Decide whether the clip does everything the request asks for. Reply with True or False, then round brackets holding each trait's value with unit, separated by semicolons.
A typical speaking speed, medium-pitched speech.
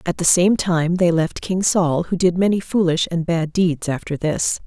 False (220 wpm; 175 Hz)